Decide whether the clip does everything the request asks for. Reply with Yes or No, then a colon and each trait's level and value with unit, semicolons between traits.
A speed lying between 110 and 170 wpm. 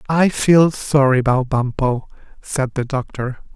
Yes: slow, 135 wpm